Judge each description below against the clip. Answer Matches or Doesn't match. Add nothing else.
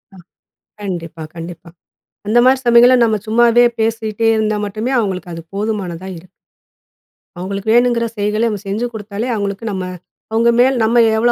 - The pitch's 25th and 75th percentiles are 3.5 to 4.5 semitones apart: Doesn't match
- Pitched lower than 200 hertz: Doesn't match